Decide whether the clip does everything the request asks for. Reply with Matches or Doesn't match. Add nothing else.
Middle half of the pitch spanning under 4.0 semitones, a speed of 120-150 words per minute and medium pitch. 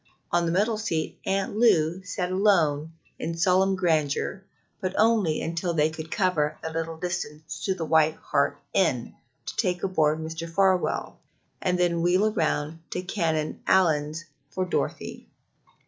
Matches